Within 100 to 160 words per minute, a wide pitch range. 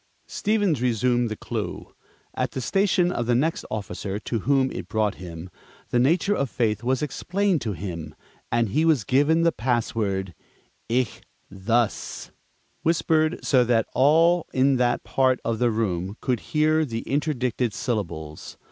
Yes: average, 145 wpm; wide, 5.9 semitones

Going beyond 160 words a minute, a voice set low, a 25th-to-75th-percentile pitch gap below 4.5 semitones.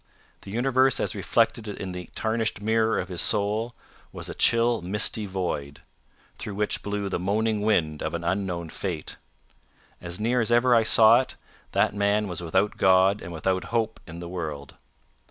Yes: average, 170 wpm; low, 100 Hz; average, 3.9 semitones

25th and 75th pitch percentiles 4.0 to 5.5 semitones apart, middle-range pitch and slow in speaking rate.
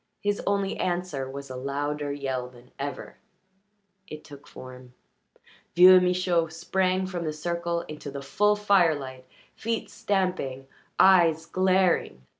Yes: average, 5.0 semitones; medium, 165 Hz; slow, 125 wpm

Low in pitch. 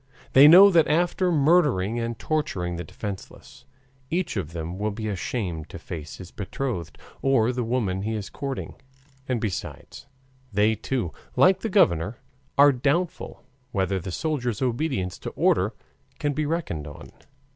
Yes: low, 115 Hz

